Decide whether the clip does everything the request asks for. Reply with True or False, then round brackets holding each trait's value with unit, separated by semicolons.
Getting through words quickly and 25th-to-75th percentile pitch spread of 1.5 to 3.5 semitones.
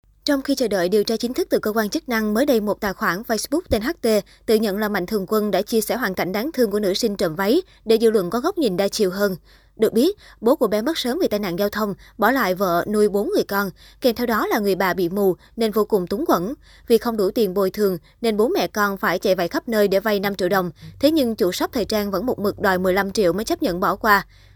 True (285 wpm; 3.1 semitones)